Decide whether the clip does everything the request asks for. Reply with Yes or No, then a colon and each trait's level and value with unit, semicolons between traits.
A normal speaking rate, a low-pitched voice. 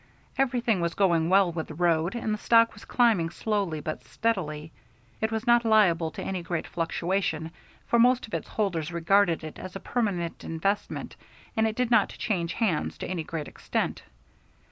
No: average, 180 wpm; medium, 185 Hz